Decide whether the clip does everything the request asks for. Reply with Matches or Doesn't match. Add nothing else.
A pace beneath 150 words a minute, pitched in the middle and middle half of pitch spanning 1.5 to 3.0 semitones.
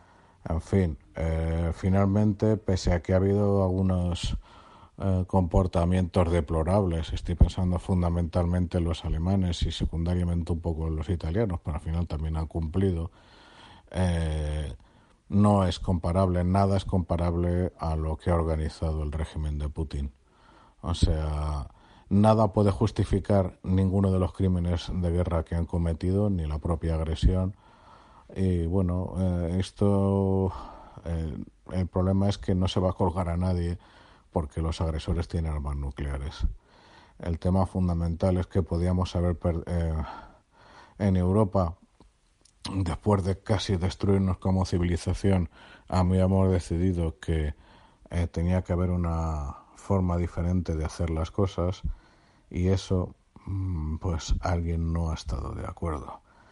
Doesn't match